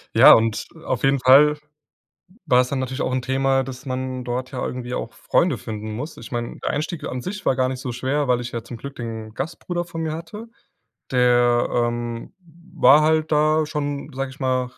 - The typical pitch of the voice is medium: No, low, 130 Hz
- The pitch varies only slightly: No, average, 3.4 semitones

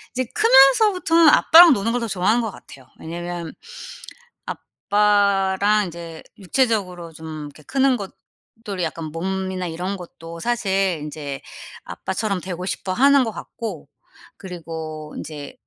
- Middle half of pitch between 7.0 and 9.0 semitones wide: No, average, 5.2 semitones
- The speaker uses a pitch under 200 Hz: Yes, high, 190 Hz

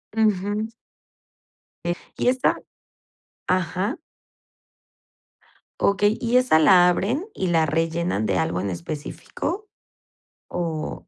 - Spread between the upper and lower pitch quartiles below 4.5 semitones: No, wide, 5.4 semitones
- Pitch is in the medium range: Yes, medium, 180 Hz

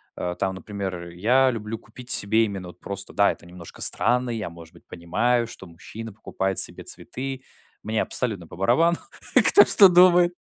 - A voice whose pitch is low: Yes, low, 105 Hz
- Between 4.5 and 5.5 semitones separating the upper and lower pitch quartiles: Yes, average, 5.1 semitones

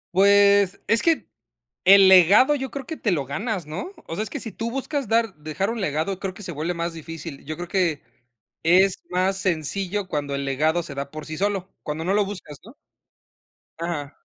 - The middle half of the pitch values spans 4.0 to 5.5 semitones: Yes, average, 4.5 semitones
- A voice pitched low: No, medium, 185 Hz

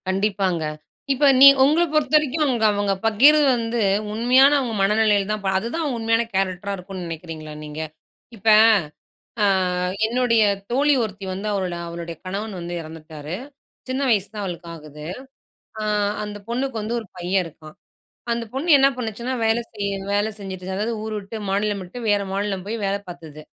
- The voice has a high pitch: Yes, high, 205 Hz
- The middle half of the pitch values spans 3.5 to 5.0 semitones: Yes, average, 4.1 semitones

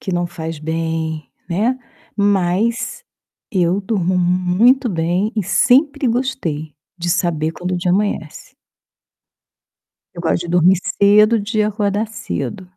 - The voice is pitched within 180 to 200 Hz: Yes, medium, 185 Hz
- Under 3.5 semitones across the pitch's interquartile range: No, average, 3.8 semitones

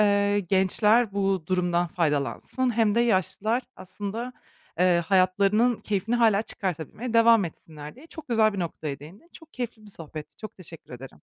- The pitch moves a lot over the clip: No, average, 4.6 semitones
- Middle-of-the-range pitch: No, high, 200 Hz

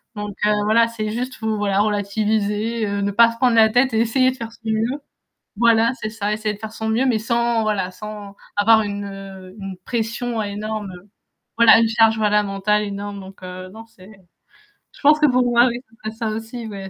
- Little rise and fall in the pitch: Yes, narrow, 2.2 semitones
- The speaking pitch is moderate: No, high, 220 Hz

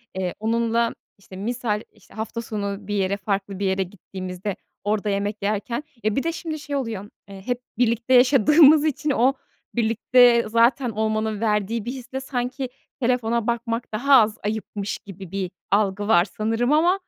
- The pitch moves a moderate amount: Yes, average, 3.3 semitones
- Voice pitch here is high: Yes, high, 220 Hz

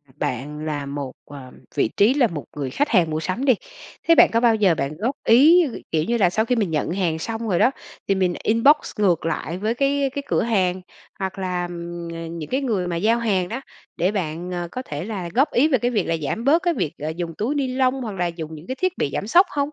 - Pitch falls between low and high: No, high, 195 Hz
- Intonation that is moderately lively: No, wide, 6.8 semitones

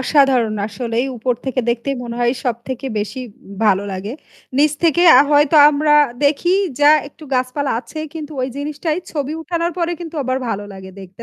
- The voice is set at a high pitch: Yes, very high, 265 Hz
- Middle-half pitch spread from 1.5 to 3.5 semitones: No, average, 4.3 semitones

